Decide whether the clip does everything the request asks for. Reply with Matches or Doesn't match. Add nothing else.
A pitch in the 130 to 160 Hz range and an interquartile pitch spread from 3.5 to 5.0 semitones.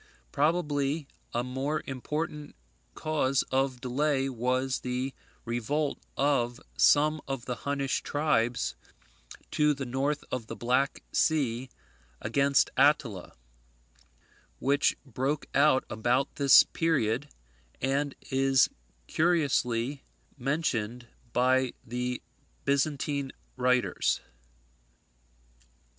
Doesn't match